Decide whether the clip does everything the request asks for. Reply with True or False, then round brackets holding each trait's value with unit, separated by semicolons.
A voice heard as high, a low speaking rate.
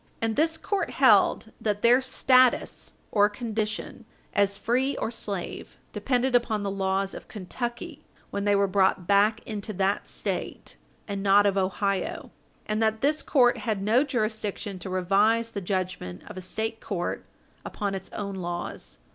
False (205 Hz; 155 wpm)